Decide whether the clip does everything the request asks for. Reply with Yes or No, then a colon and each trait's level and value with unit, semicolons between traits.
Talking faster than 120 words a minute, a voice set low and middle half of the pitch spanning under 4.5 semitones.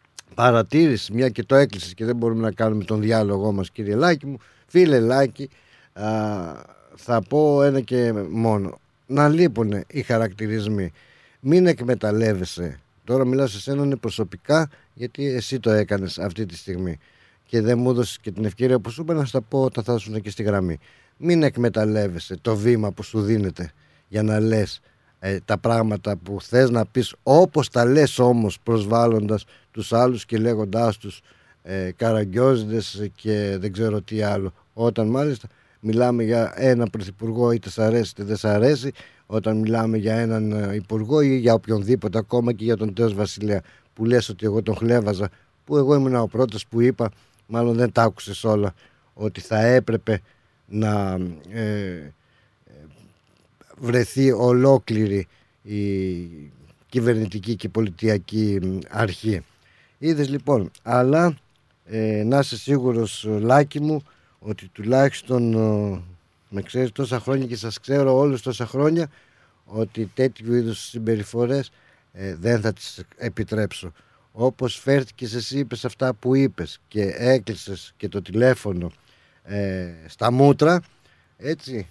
Yes: average, 145 wpm; low, 115 Hz; average, 3.5 semitones